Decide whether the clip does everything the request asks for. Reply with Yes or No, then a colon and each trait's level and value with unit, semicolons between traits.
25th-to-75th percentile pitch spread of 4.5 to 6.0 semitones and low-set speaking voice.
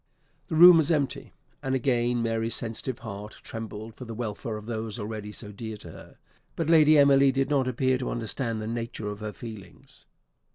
No: average, 3.5 semitones; low, 115 Hz